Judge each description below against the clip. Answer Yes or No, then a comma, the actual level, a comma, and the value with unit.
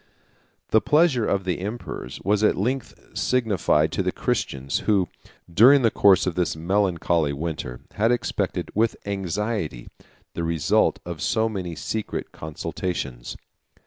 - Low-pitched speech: Yes, very low, 95 Hz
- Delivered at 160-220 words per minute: No, average, 140 wpm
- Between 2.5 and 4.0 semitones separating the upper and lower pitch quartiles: No, average, 4.9 semitones